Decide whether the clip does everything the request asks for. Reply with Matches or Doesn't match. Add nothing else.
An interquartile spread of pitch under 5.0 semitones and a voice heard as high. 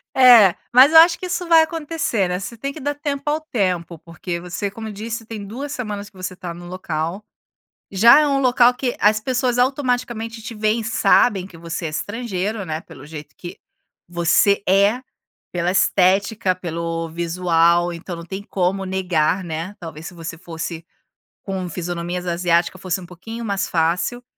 Doesn't match